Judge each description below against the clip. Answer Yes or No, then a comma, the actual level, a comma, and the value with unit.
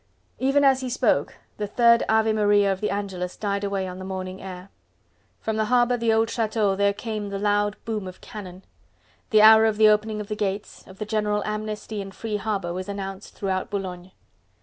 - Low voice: No, high, 210 Hz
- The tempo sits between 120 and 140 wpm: No, fast, 205 wpm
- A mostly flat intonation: Yes, narrow, 2.1 semitones